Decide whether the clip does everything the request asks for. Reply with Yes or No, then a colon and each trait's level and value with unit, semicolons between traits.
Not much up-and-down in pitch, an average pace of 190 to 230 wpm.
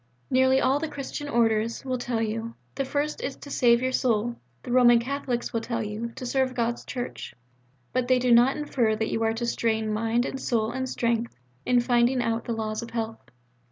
Yes: narrow, 2.2 semitones; fast, 205 wpm